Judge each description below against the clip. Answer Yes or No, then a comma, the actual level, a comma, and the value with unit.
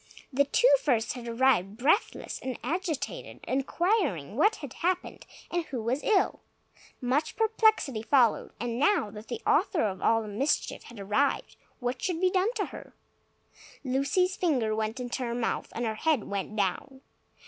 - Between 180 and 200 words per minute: No, average, 160 wpm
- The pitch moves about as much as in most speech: No, wide, 6.8 semitones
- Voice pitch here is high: Yes, very high, 260 Hz